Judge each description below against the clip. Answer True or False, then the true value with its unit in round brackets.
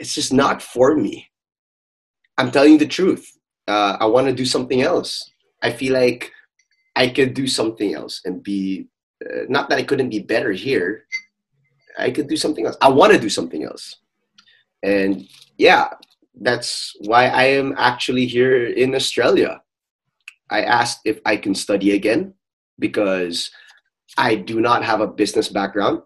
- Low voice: True (130 Hz)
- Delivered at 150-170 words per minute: True (160 wpm)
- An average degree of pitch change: False (6.0 semitones)